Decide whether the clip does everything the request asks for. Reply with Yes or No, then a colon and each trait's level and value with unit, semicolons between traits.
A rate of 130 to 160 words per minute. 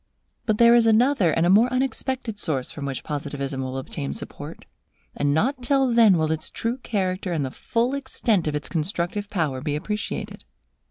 No: average, 180 wpm